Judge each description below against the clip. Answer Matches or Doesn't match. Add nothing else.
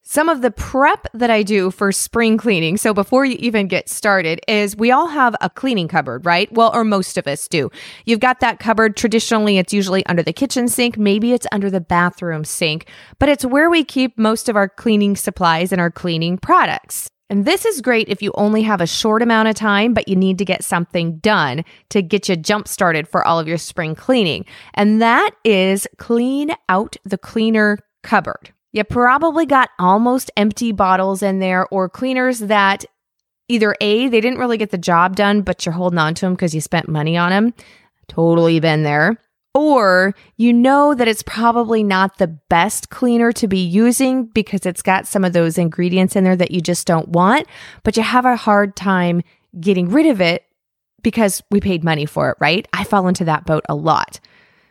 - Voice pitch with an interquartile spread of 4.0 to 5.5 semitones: Matches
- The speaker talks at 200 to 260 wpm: Matches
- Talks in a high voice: Matches